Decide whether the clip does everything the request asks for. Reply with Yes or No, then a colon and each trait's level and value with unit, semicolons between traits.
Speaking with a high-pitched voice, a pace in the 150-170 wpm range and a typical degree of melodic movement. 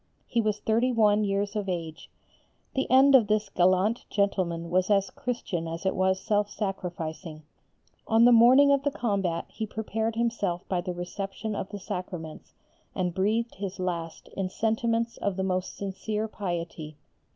Yes: high, 200 Hz; average, 160 wpm; average, 3.5 semitones